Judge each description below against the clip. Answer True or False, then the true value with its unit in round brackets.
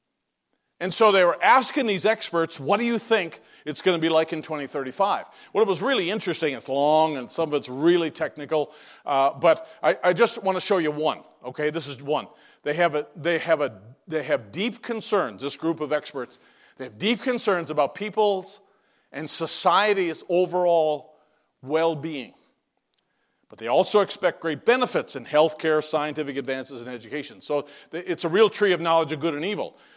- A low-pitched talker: False (165 Hz)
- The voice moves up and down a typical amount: True (4.7 semitones)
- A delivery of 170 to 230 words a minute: True (185 wpm)